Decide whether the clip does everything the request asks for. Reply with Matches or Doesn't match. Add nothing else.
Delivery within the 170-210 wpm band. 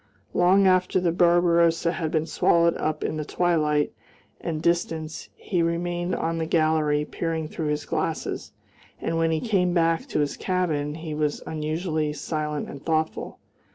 Doesn't match